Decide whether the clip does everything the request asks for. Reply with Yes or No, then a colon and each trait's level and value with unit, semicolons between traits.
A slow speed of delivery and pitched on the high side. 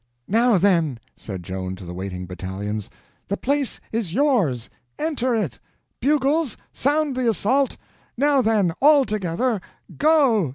Yes: slow, 115 wpm; high, 215 Hz